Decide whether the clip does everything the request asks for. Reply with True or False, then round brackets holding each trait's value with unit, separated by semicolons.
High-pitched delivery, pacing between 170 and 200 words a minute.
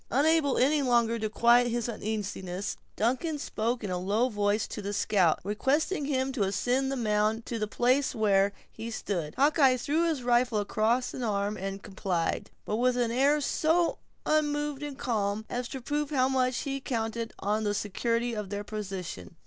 True (235 Hz; 180 wpm)